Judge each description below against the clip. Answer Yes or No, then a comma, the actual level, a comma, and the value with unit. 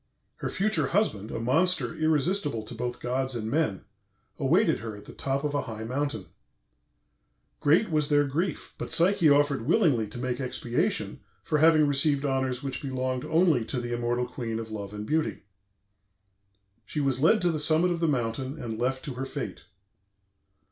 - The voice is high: No, low, 135 Hz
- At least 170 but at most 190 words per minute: Yes, average, 175 wpm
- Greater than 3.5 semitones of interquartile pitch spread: Yes, average, 4.3 semitones